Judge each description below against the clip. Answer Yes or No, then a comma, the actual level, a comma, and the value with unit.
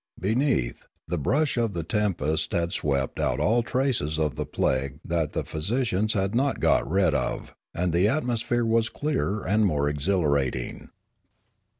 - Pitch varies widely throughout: Yes, wide, 7.2 semitones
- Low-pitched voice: Yes, very low, 95 Hz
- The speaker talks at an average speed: Yes, average, 160 wpm